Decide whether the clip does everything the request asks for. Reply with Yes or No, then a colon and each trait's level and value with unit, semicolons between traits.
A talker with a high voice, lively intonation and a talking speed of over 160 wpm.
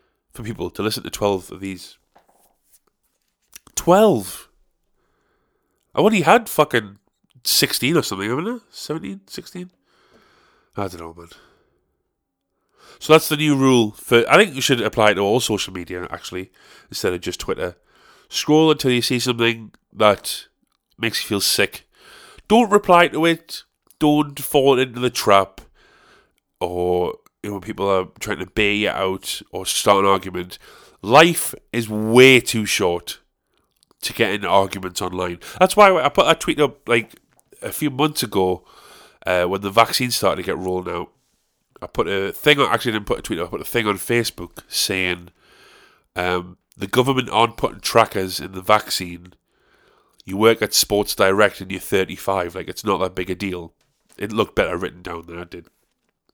No: low, 105 Hz; wide, 5.8 semitones; average, 175 wpm